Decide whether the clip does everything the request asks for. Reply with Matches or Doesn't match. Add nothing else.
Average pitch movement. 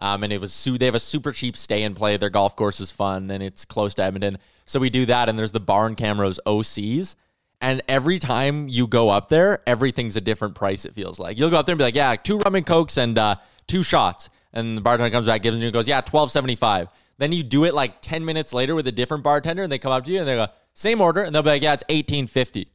Doesn't match